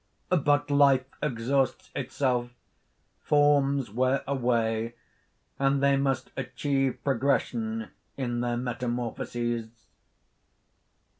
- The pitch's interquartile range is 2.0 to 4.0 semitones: Yes, narrow, 2.6 semitones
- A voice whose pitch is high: No, low, 135 Hz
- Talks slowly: Yes, slow, 80 wpm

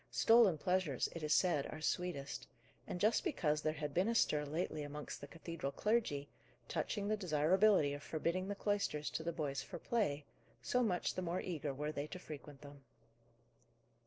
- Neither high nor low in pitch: Yes, medium, 160 Hz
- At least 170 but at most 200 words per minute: Yes, average, 180 wpm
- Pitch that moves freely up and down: No, average, 4.2 semitones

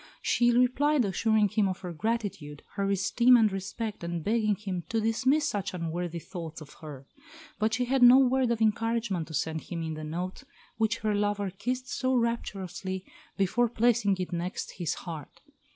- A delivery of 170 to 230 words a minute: Yes, average, 175 wpm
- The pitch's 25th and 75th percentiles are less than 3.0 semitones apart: No, average, 4.9 semitones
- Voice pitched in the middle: No, high, 205 Hz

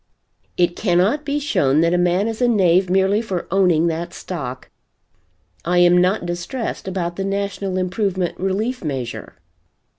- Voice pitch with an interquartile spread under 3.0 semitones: Yes, narrow, 2.4 semitones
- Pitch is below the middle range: No, medium, 185 Hz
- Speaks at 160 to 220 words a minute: No, average, 150 wpm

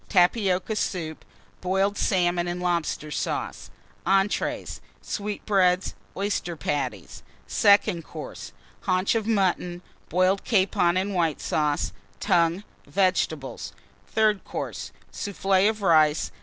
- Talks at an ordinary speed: No, slow, 100 wpm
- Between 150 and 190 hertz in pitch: Yes, medium, 185 Hz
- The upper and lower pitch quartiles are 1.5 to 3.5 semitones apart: Yes, average, 2.7 semitones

